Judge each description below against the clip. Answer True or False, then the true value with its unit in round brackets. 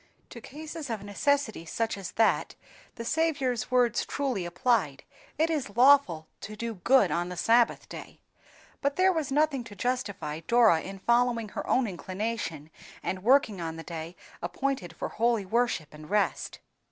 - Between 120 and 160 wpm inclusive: True (155 wpm)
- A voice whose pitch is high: True (225 Hz)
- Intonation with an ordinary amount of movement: False (6.3 semitones)